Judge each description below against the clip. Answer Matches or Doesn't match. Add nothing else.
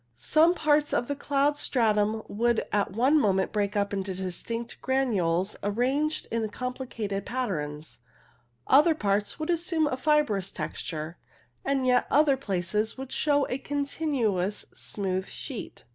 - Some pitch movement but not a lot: Doesn't match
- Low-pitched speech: Doesn't match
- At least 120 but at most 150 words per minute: Matches